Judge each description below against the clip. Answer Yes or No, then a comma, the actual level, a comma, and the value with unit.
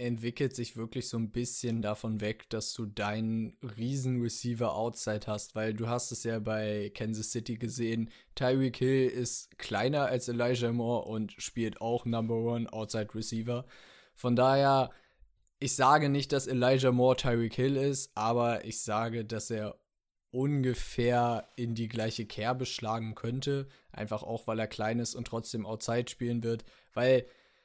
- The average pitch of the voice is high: No, low, 120 Hz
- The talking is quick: No, average, 155 wpm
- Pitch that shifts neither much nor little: No, narrow, 2.1 semitones